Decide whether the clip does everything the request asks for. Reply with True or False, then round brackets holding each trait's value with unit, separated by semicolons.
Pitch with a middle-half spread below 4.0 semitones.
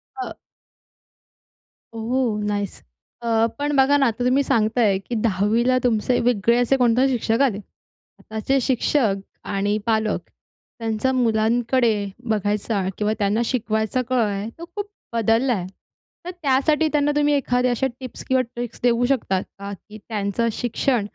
True (3.3 semitones)